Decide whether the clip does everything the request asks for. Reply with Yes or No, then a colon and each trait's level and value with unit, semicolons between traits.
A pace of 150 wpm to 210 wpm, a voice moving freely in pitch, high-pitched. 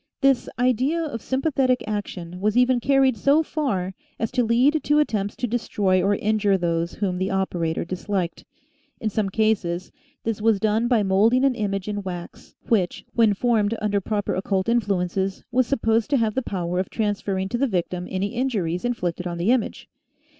No: average, 180 wpm; average, 4.4 semitones; high, 210 Hz